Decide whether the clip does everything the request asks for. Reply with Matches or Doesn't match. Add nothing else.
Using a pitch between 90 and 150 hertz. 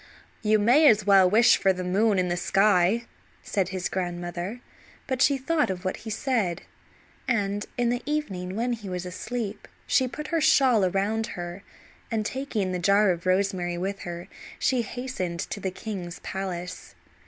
Doesn't match